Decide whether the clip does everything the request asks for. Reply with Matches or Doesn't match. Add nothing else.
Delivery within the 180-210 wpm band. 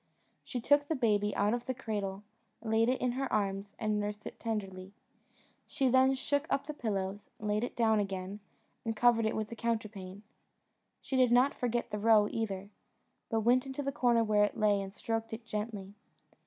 Matches